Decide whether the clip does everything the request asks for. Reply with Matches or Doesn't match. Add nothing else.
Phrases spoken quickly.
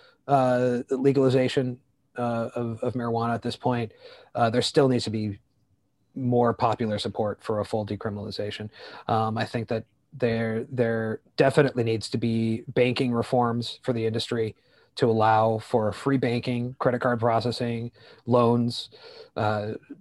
Doesn't match